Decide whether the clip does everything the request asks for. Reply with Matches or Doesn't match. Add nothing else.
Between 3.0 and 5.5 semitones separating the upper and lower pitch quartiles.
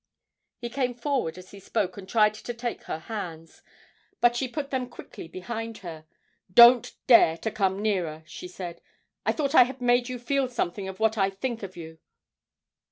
Matches